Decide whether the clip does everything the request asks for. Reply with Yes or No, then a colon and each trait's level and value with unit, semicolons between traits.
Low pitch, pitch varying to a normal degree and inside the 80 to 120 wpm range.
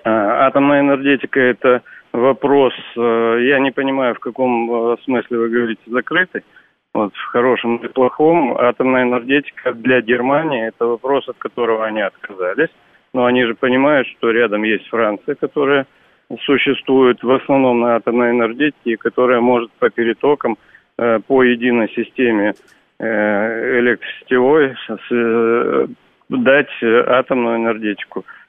No: low, 125 Hz; narrow, 2.3 semitones; average, 115 wpm